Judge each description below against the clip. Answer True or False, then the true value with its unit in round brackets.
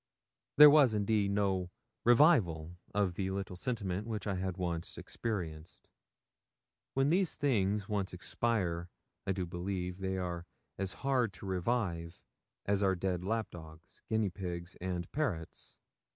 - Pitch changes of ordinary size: True (3.7 semitones)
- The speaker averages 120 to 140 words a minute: True (135 wpm)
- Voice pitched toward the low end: True (95 Hz)